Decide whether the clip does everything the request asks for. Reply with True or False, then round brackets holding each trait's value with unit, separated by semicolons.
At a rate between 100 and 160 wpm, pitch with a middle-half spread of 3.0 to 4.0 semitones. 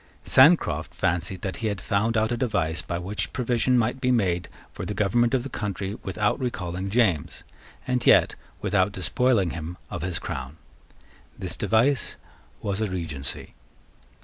False (155 wpm; 4.9 semitones)